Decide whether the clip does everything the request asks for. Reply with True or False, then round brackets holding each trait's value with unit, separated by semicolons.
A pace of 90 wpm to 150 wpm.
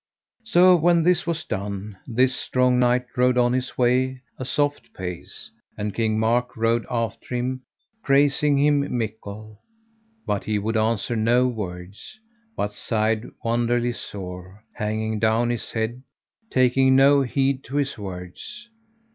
True (140 wpm)